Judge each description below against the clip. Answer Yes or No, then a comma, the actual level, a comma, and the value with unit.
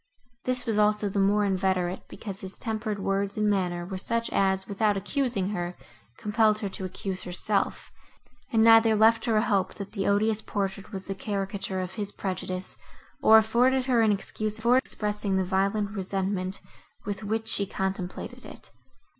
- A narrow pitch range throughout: Yes, narrow, 2.3 semitones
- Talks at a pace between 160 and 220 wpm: Yes, average, 170 wpm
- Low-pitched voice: No, high, 200 Hz